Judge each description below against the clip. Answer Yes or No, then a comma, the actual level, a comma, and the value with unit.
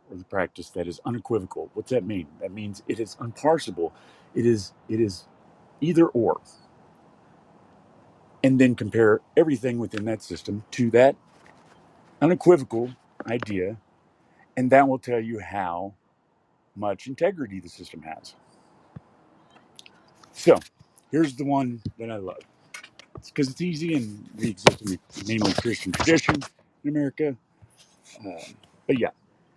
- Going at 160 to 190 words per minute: No, slow, 135 wpm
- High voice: No, low, 115 Hz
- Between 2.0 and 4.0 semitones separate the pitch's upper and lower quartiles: No, average, 4.7 semitones